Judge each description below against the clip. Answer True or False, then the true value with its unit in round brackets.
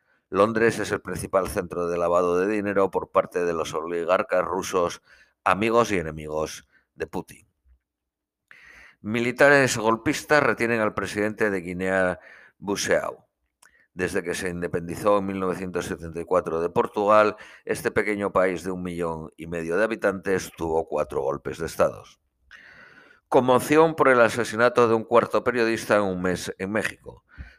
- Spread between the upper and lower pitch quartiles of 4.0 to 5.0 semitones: True (4.5 semitones)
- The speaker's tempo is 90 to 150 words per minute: True (140 wpm)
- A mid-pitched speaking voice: False (95 Hz)